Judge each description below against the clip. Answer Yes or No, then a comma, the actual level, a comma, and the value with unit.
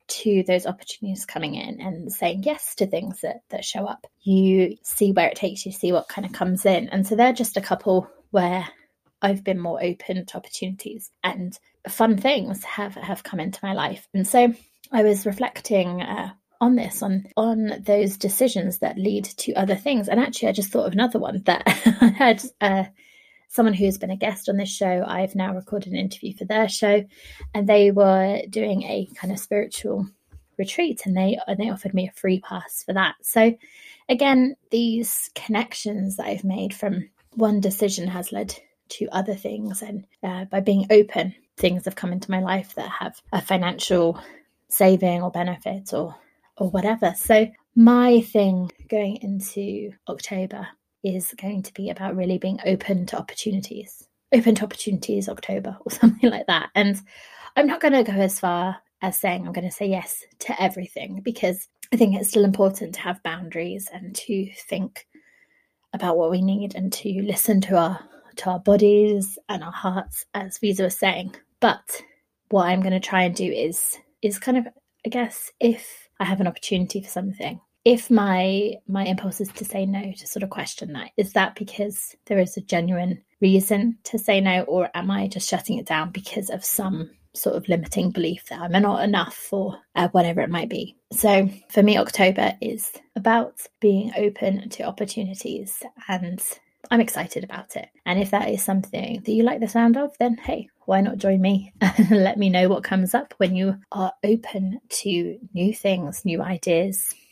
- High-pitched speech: Yes, high, 200 Hz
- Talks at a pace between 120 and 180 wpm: No, average, 190 wpm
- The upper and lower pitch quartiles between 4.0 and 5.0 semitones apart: No, narrow, 2.6 semitones